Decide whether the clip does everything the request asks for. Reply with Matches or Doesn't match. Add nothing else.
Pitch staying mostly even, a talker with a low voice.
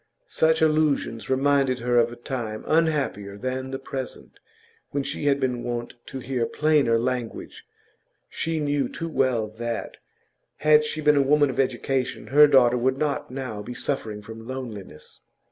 Doesn't match